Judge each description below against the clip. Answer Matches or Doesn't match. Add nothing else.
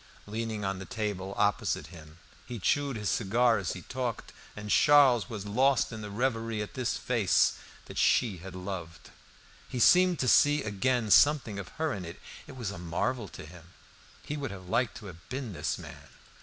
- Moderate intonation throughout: Matches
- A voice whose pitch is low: Matches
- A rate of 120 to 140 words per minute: Doesn't match